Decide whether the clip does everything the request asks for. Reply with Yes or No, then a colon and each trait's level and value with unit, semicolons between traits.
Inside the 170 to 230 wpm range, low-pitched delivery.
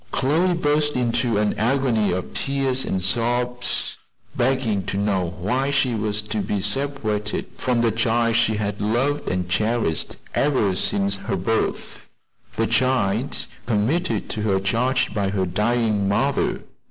No: average, 140 wpm; low, 115 Hz